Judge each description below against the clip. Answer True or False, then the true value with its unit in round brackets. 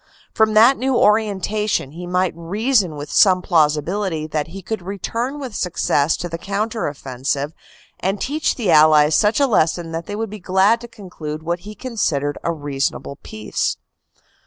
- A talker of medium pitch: True (180 Hz)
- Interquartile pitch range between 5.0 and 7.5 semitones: True (5.6 semitones)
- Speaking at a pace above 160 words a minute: True (175 wpm)